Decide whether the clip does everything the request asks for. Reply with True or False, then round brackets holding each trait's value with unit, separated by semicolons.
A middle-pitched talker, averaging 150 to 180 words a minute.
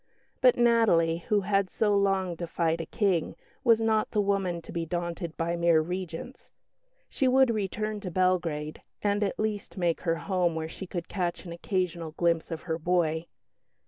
True (180 Hz; 175 wpm)